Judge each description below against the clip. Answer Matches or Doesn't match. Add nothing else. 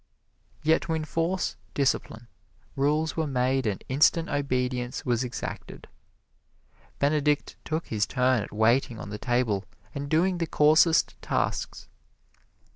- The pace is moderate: Doesn't match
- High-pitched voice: Doesn't match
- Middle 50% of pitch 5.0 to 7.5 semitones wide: Doesn't match